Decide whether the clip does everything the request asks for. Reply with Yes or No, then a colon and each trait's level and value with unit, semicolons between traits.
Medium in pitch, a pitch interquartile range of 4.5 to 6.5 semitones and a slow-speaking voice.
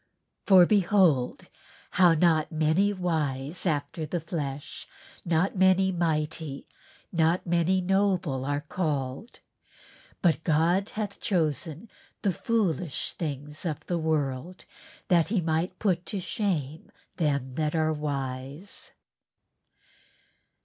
No: medium, 165 Hz; average, 3.7 semitones; slow, 110 wpm